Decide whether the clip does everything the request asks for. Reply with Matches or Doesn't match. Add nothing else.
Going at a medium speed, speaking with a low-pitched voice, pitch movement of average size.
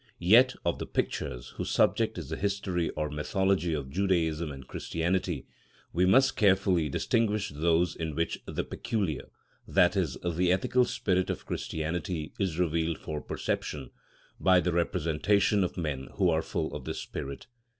Matches